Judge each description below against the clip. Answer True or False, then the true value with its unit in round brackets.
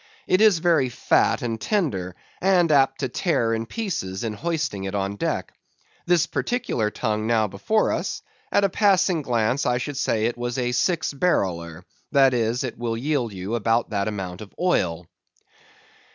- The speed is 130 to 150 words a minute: False (170 wpm)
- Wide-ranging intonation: True (7.1 semitones)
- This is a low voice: True (120 Hz)